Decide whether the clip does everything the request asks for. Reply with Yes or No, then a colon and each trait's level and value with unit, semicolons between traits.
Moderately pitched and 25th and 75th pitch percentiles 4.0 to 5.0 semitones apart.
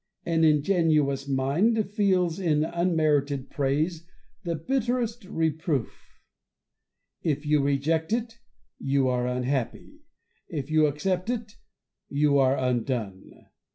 Yes: medium, 155 Hz; average, 4.7 semitones